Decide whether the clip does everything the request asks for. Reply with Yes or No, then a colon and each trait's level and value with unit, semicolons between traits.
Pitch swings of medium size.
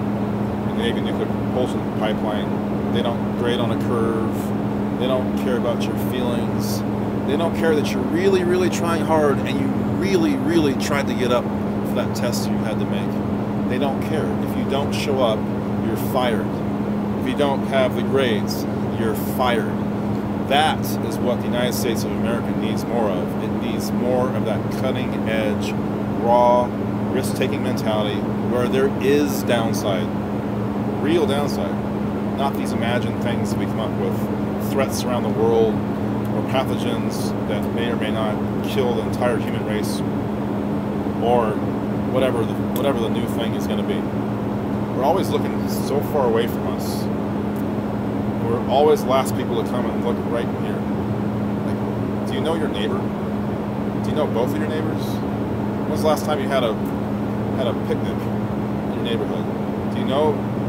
No: narrow, 0.8 semitones